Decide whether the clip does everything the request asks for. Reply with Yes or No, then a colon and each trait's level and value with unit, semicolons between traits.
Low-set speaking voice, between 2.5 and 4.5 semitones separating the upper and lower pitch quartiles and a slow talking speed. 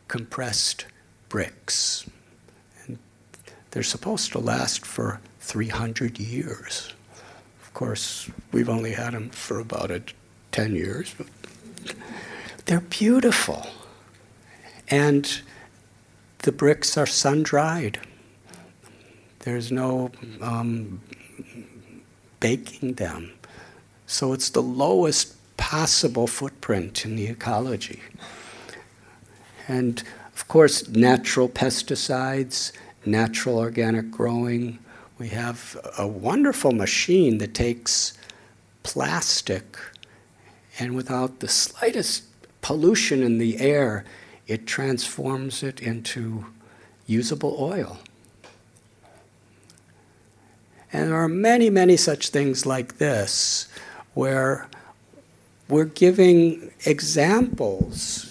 Yes: low, 120 Hz; average, 3.5 semitones; slow, 90 wpm